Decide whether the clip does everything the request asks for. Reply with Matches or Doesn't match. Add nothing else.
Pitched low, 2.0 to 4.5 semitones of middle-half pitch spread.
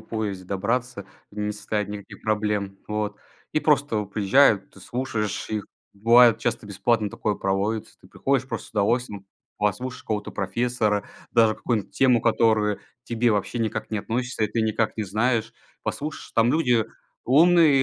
Matches